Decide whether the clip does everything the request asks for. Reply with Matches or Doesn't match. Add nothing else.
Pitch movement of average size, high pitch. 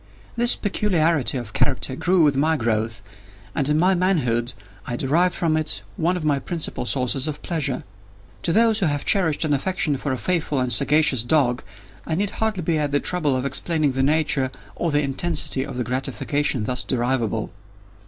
Doesn't match